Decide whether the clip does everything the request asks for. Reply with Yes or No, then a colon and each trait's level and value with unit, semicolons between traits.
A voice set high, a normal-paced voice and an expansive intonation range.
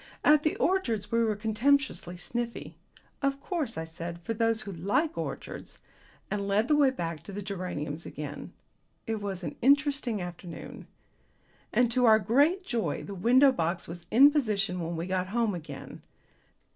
Yes: high, 215 Hz; average, 170 wpm; wide, 6.6 semitones